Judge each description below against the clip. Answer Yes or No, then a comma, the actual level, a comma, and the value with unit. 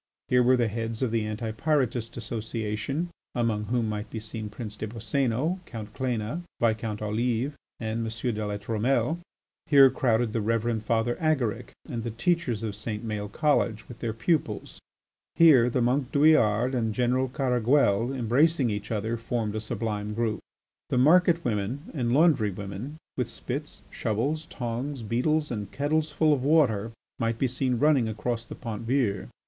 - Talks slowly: No, average, 165 wpm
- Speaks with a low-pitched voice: Yes, low, 120 Hz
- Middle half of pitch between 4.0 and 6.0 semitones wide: No, average, 3.6 semitones